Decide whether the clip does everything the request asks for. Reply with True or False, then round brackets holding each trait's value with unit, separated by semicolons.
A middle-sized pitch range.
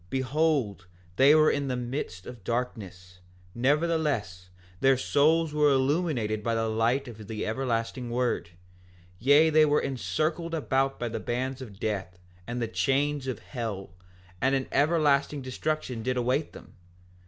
True (4.4 semitones)